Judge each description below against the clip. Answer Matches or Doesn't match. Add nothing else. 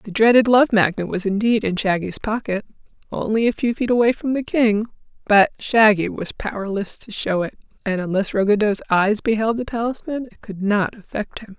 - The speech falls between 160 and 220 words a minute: Matches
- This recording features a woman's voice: Matches